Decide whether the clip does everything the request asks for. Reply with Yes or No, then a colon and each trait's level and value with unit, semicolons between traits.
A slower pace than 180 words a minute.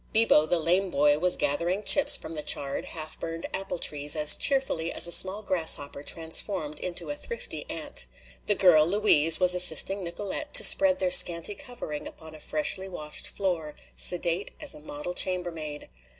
Yes: average, 170 wpm